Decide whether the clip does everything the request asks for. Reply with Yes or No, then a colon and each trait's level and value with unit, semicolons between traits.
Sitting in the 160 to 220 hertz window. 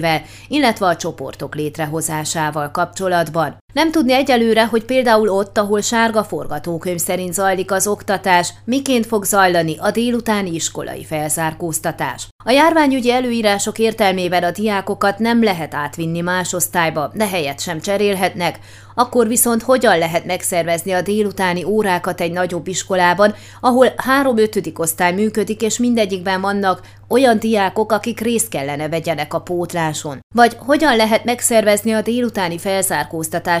Yes: high, 190 Hz